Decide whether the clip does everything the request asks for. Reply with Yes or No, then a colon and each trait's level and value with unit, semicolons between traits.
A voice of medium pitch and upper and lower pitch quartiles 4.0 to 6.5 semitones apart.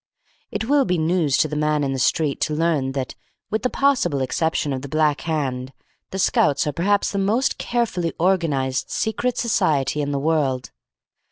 Yes: medium, 155 Hz; wide, 5.5 semitones